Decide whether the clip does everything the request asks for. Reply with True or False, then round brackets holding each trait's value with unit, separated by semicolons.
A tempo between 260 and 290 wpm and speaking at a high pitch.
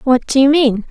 True (265 wpm; 260 Hz)